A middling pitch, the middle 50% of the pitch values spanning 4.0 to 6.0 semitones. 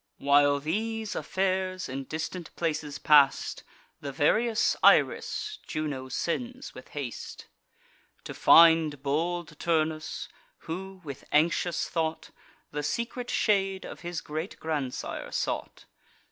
Yes: medium, 160 Hz; average, 4.3 semitones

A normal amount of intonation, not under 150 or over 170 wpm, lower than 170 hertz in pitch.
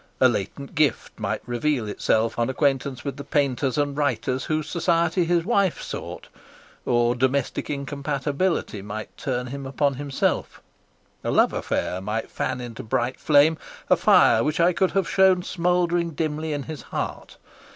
Yes: average, 4.3 semitones; average, 155 wpm; medium, 140 Hz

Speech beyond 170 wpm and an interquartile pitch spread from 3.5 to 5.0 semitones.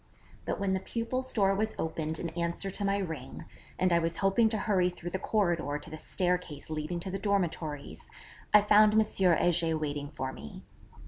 Yes: average, 190 wpm; average, 4.0 semitones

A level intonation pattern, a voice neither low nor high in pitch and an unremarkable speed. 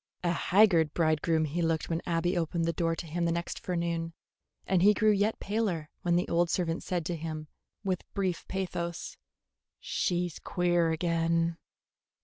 Yes: narrow, 1.4 semitones; medium, 170 Hz; average, 165 wpm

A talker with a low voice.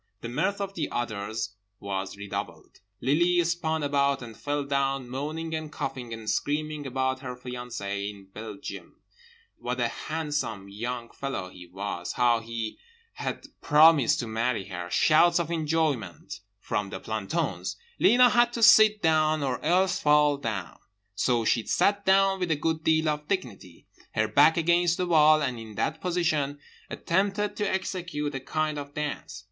No: medium, 145 Hz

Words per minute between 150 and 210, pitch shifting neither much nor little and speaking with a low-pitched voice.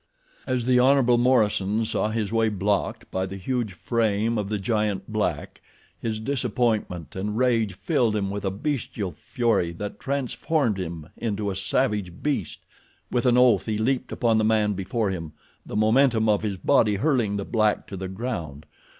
Yes: average, 170 wpm; average, 3.6 semitones; low, 110 Hz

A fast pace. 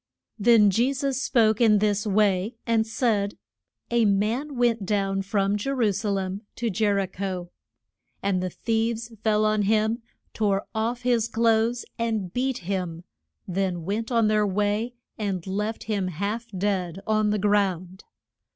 No: average, 155 wpm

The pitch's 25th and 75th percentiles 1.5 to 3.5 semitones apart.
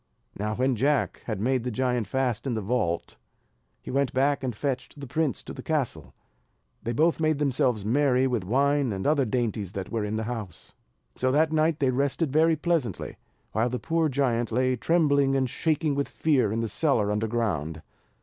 No: average, 4.2 semitones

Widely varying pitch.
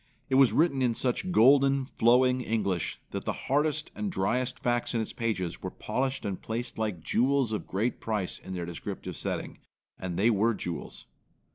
No: average, 4.5 semitones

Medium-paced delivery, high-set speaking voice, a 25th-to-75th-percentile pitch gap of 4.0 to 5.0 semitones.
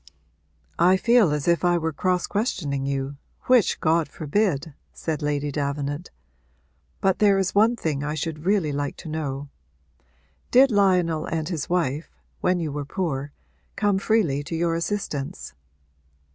No: average, 145 wpm; medium, 165 Hz; average, 4.7 semitones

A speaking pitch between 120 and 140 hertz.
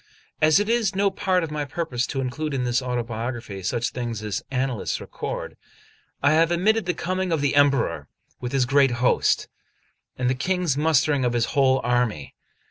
Yes: low, 135 Hz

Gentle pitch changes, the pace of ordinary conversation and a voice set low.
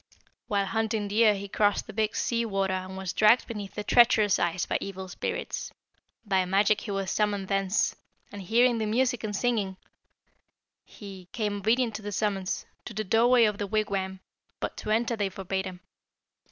No: narrow, 2.3 semitones; average, 180 wpm; high, 205 Hz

